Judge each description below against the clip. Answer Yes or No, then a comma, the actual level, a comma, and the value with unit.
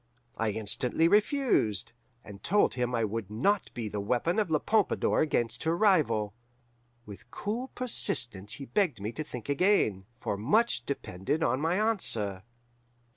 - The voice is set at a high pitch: No, low, 125 Hz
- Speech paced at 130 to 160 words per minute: Yes, average, 150 wpm